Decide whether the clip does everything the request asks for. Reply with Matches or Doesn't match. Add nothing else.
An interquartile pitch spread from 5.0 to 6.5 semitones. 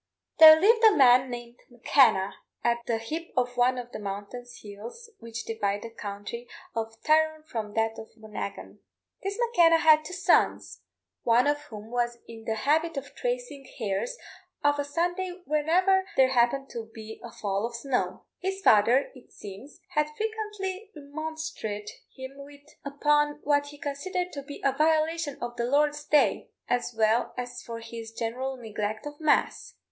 Matches